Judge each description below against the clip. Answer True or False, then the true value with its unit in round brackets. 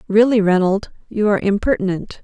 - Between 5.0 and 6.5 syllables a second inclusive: True (5.8 syllables/s)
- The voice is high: True (205 Hz)